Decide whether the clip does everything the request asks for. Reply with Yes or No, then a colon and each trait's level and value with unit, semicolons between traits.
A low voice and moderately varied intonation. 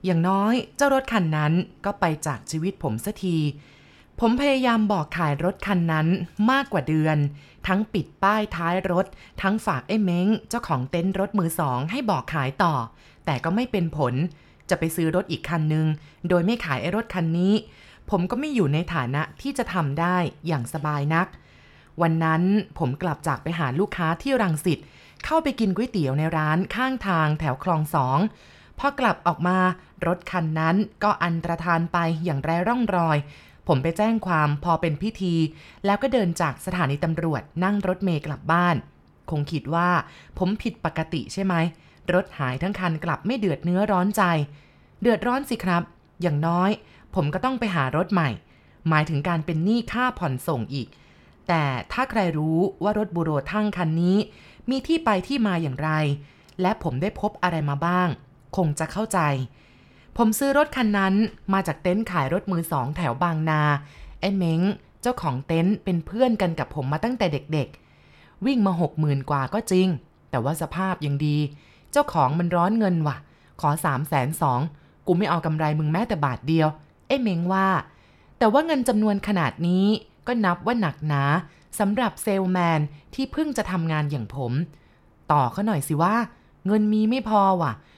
No: medium, 175 Hz; average, 4.7 semitones